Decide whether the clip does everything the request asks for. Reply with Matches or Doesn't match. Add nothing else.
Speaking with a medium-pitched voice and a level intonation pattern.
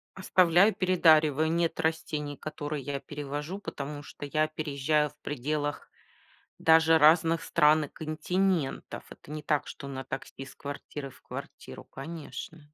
Matches